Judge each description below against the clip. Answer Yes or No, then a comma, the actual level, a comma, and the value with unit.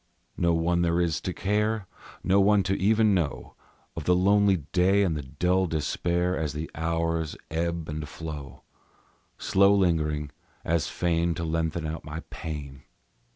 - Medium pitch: No, very low, 85 Hz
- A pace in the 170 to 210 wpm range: No, average, 155 wpm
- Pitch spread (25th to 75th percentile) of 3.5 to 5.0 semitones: No, average, 3.1 semitones